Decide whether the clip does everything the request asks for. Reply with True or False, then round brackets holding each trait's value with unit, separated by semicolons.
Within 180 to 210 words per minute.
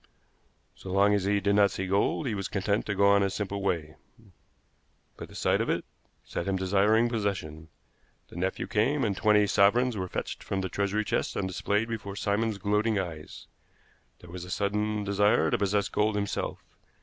True (185 wpm)